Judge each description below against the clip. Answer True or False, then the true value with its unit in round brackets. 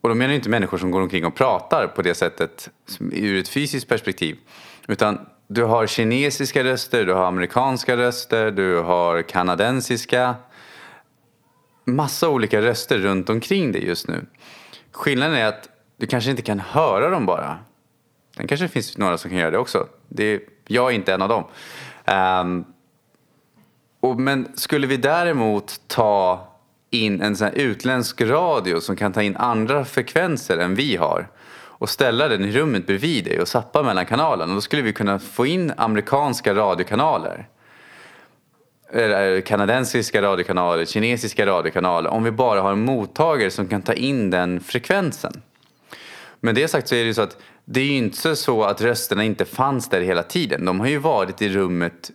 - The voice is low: True (110 Hz)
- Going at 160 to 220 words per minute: True (165 wpm)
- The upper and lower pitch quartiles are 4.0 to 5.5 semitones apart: True (4.7 semitones)